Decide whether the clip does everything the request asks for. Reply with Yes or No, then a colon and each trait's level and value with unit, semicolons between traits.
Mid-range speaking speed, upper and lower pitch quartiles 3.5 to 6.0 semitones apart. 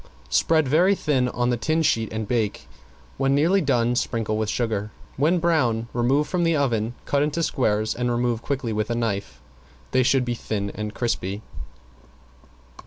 Yes: average, 170 wpm; average, 4.4 semitones